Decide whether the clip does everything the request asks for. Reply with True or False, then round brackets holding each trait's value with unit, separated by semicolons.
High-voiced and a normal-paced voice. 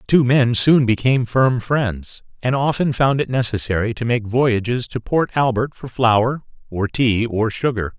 False (120 Hz; 180 wpm)